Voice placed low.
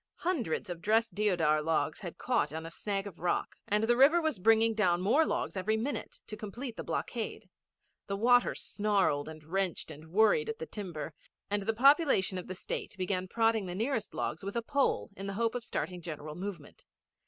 No: high, 205 Hz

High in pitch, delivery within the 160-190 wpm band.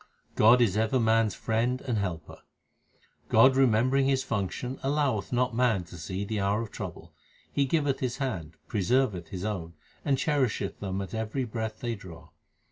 No: low, 110 Hz; average, 170 wpm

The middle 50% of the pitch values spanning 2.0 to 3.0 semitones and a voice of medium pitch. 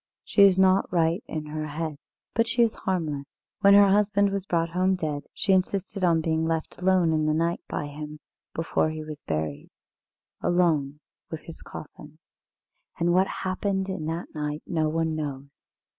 No: average, 3.6 semitones; medium, 165 Hz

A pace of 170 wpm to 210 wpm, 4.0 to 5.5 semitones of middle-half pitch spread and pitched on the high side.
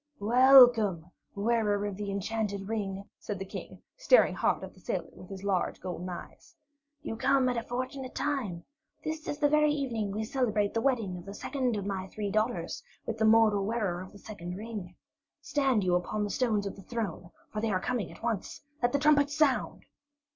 Yes: average, 190 wpm; average, 4.3 semitones; high, 215 Hz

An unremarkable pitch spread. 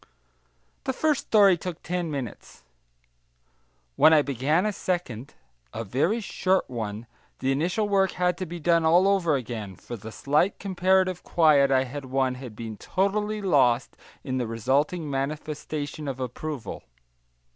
No: wide, 5.9 semitones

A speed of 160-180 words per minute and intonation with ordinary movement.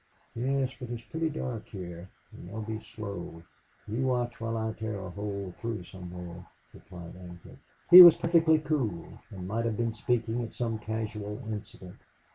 Yes: average, 165 wpm; average, 4.2 semitones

